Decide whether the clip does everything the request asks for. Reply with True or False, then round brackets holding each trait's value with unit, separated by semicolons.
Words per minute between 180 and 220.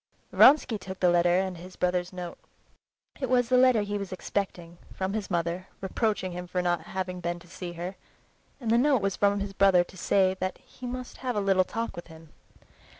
True (200 wpm)